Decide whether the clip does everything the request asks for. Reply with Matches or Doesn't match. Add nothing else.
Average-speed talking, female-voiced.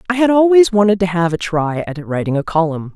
Doesn't match